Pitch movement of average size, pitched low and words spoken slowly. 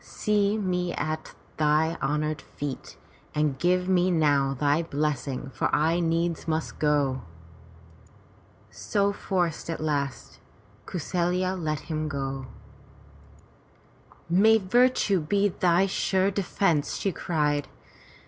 No: average, 3.8 semitones; medium, 165 Hz; slow, 110 wpm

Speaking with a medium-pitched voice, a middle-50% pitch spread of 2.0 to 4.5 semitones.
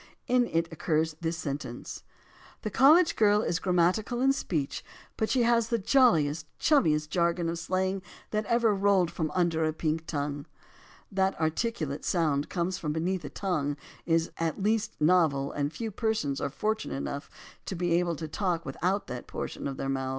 No: medium, 170 Hz; average, 5.1 semitones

